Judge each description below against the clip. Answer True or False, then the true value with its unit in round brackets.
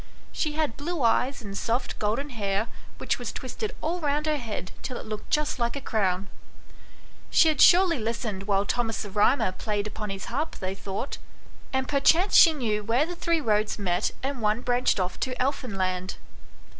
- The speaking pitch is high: True (235 Hz)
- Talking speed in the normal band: True (180 wpm)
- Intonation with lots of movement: True (5.8 semitones)